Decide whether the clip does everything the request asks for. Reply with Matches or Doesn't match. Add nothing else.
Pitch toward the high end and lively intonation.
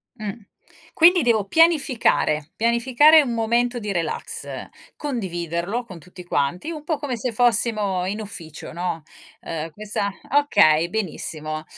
Matches